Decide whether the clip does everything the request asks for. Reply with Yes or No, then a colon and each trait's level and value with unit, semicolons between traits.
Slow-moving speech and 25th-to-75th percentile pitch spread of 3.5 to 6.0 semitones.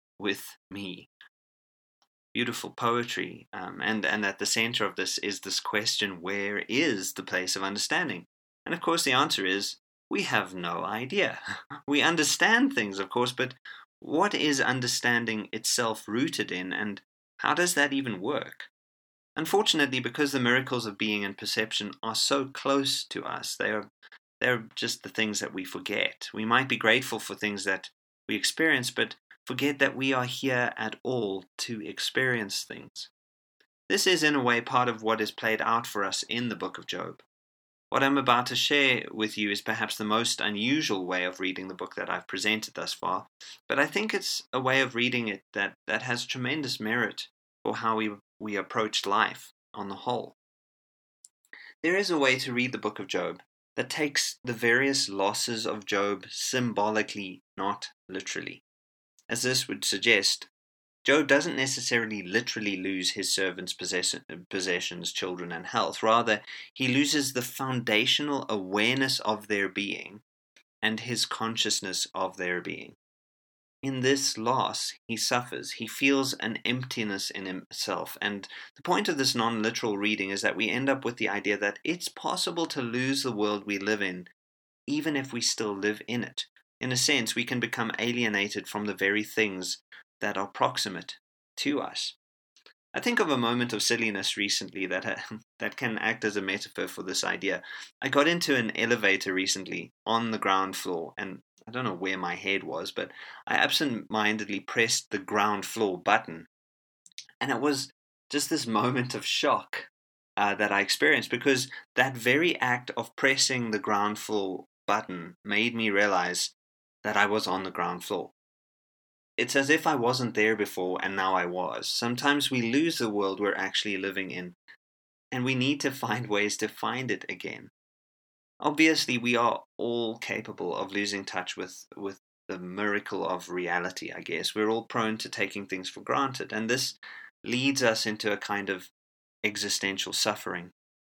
No: average, 170 wpm; average, 4.3 semitones